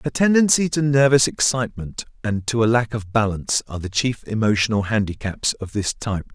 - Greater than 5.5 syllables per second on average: Yes, 5.7 syllables/s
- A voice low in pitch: Yes, low, 115 Hz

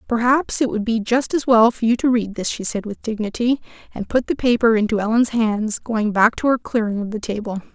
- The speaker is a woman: Yes, female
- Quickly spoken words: Yes, fast, 240 wpm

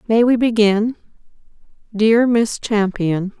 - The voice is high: Yes, high, 220 Hz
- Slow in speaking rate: Yes, slow, 105 wpm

